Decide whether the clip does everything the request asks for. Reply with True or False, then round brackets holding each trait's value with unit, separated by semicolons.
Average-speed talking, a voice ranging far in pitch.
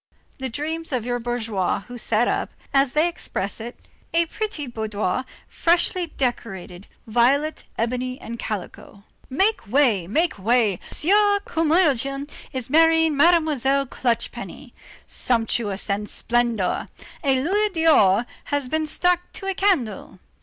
False (130 wpm; 6.1 semitones)